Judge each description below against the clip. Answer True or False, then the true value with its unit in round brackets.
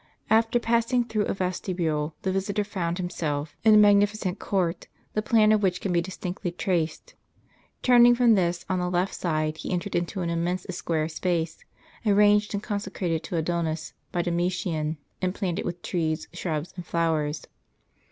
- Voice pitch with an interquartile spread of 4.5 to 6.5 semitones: False (3.5 semitones)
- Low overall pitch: False (180 Hz)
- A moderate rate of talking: True (160 wpm)